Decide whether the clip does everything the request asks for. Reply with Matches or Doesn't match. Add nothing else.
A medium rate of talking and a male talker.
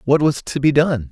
Doesn't match